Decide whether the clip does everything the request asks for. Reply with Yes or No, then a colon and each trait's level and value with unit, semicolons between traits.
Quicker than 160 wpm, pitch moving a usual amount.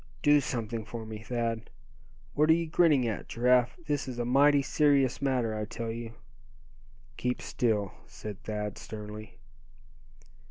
No: average, 145 wpm; average, 3.9 semitones